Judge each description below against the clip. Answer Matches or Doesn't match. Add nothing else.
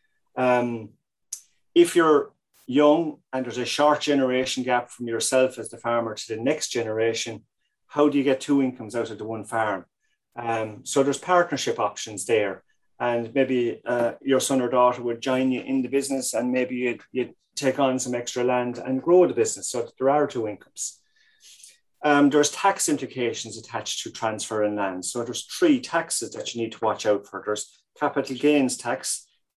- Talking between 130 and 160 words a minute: Doesn't match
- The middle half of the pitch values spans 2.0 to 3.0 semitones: Doesn't match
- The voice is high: Doesn't match